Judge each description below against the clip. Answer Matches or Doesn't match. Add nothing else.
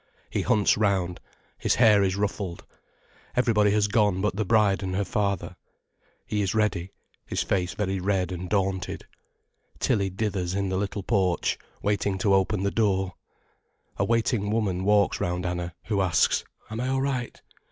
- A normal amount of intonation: Doesn't match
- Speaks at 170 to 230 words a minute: Doesn't match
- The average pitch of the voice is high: Doesn't match